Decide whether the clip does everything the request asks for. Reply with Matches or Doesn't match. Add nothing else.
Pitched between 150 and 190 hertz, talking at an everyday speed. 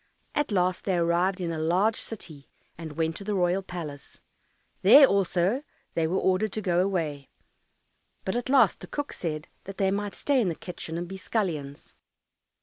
Matches